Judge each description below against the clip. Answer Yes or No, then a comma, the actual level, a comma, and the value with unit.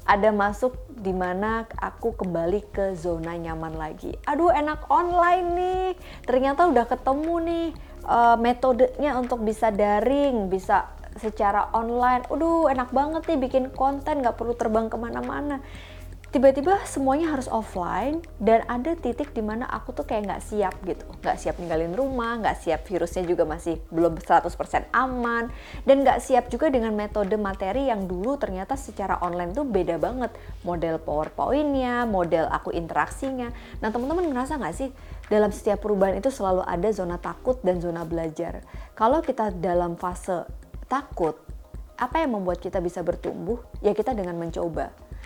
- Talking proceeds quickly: Yes, fast, 150 wpm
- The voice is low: No, high, 225 Hz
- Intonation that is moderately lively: No, wide, 6.6 semitones